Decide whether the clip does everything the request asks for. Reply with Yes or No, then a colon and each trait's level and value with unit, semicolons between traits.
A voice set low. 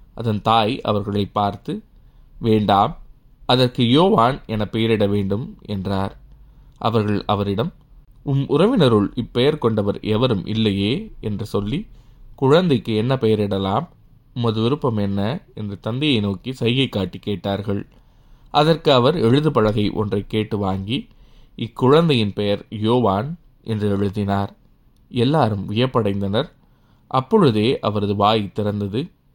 Yes: low, 110 Hz